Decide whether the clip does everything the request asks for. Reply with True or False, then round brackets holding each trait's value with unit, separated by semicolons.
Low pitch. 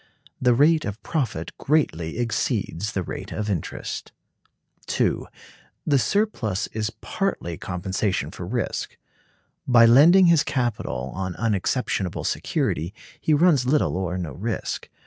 True (110 Hz)